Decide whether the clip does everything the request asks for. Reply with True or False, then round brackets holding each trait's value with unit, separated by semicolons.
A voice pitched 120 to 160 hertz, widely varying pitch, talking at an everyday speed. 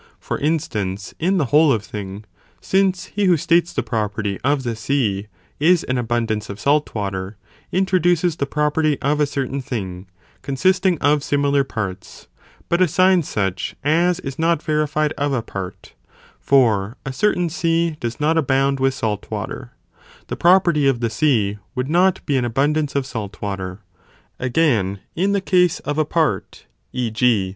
True (140 Hz; 6.6 semitones; 165 wpm)